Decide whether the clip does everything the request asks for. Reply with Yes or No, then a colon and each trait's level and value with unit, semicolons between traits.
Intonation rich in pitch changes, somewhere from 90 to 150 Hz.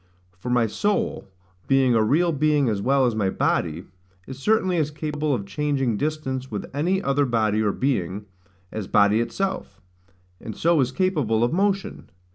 Yes: wide, 5.9 semitones; low, 135 Hz